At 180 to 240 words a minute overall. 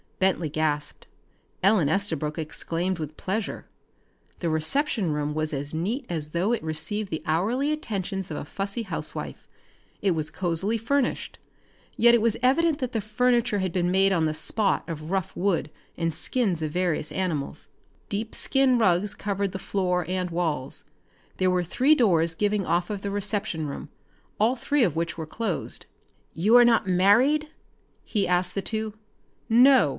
No: average, 165 wpm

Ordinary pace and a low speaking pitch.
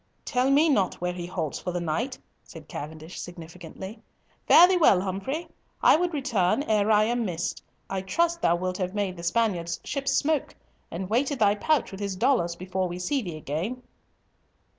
No: average, 185 wpm; high, 195 Hz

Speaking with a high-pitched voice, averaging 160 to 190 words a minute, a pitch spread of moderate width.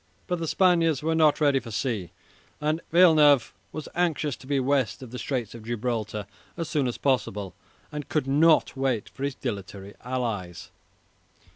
No: low, 135 Hz; average, 165 wpm; average, 5.0 semitones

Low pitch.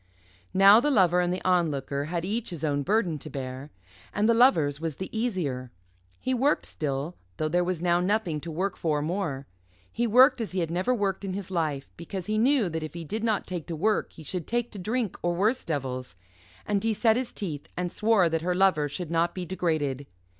No: medium, 180 Hz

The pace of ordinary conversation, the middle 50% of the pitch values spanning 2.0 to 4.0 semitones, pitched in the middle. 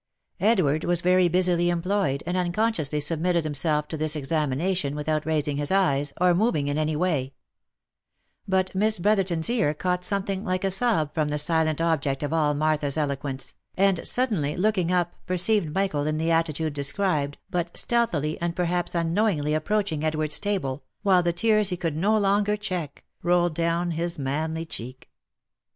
Yes: average, 160 wpm; average, 3.7 semitones; medium, 170 Hz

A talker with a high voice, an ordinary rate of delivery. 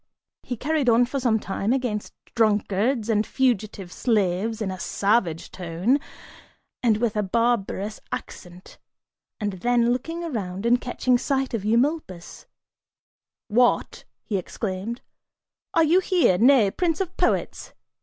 No: high, 230 Hz; slow, 130 wpm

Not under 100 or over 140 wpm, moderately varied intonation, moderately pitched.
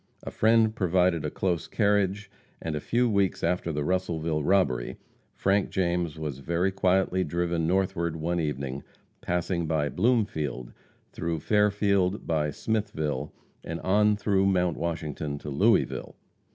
No: slow, 135 wpm; average, 3.9 semitones; very low, 85 Hz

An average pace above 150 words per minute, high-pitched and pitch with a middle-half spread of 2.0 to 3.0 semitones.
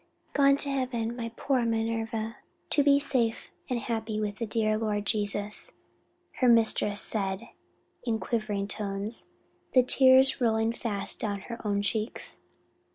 No: average, 145 wpm; high, 225 Hz; narrow, 2.5 semitones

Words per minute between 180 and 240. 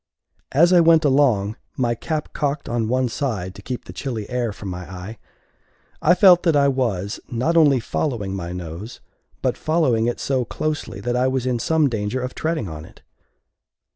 Yes: average, 185 wpm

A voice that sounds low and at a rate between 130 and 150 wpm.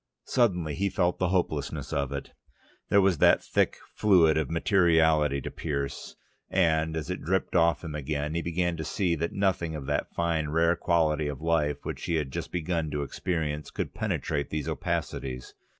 No: very low, 80 Hz; average, 180 wpm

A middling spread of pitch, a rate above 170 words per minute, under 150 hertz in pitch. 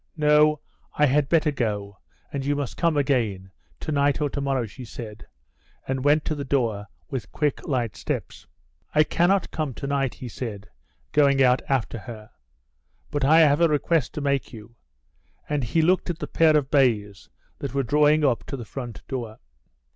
Yes: average, 4.0 semitones; average, 185 wpm; medium, 140 Hz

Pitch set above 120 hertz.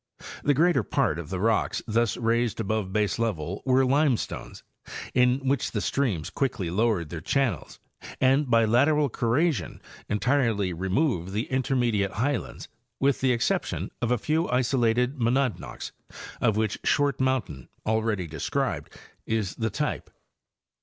No: low, 115 Hz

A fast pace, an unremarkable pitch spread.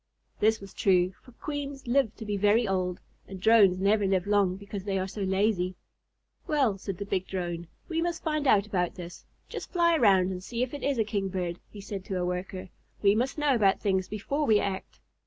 Yes: fast, 210 wpm; average, 3.7 semitones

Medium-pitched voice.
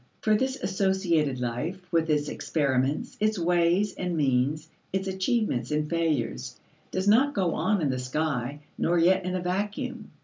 Yes: medium, 170 Hz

